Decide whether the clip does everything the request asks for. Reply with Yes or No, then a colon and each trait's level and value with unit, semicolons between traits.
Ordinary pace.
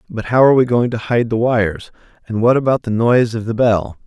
No: fast, 250 wpm